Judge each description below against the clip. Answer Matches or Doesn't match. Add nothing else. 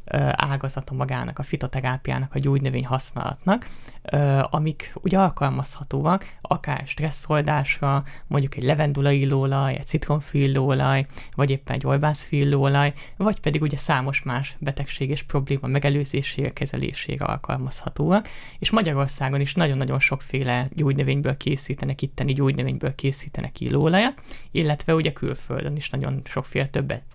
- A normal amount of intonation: Doesn't match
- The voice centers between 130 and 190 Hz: Matches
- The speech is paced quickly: Doesn't match